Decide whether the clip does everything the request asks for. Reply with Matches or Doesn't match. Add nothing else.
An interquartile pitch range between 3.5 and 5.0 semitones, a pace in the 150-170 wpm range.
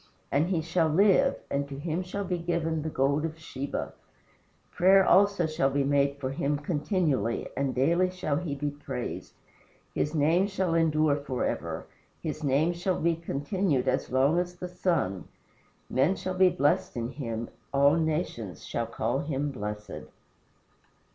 Matches